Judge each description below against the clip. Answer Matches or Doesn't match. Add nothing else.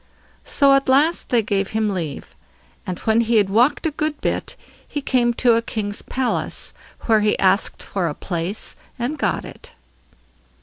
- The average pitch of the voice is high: Matches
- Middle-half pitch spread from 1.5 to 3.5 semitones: Doesn't match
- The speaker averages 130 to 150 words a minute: Doesn't match